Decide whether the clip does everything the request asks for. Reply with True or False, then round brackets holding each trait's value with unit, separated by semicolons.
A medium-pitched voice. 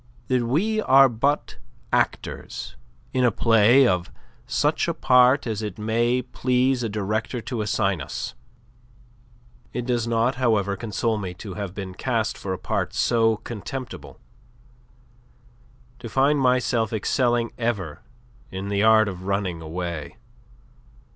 False (115 Hz)